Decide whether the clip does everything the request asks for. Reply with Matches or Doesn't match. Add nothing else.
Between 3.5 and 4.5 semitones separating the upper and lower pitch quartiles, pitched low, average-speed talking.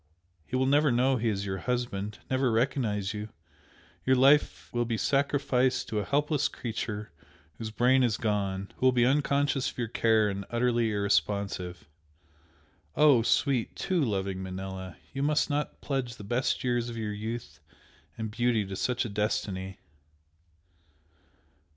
Matches